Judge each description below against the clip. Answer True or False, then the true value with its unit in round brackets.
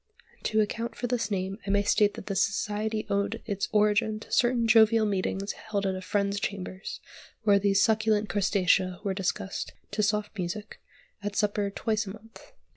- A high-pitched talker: True (205 Hz)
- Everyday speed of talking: True (175 wpm)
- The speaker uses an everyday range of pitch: False (1.7 semitones)